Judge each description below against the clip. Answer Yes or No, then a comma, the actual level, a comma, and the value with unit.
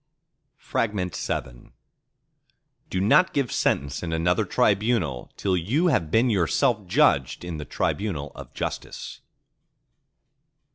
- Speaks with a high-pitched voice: No, very low, 95 Hz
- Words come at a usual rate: No, slow, 105 wpm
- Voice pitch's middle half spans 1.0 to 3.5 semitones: No, wide, 5.5 semitones